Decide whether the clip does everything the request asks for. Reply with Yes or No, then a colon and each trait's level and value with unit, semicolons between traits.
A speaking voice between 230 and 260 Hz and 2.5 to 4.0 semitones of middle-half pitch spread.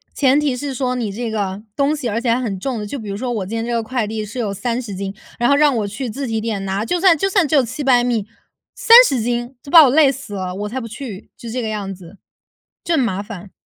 No: high, 235 Hz; average, 4.4 semitones